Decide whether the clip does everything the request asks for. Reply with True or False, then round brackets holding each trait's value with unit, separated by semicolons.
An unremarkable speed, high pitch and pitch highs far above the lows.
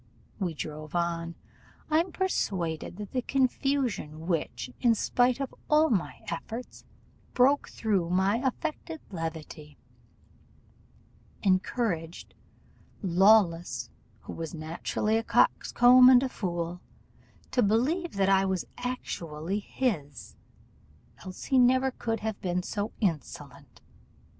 False (110 wpm; 200 Hz; 6.9 semitones)